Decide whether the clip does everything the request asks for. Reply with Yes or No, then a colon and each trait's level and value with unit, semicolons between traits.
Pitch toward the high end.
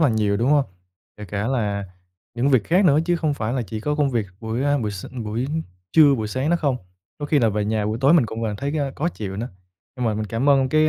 No: low, 125 Hz